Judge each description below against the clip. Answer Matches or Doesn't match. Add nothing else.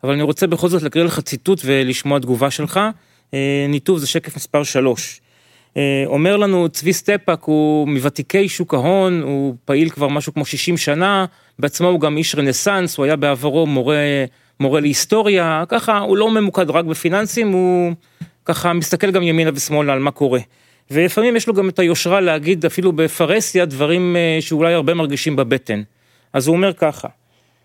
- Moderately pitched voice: Matches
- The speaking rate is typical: Doesn't match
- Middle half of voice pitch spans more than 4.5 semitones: Doesn't match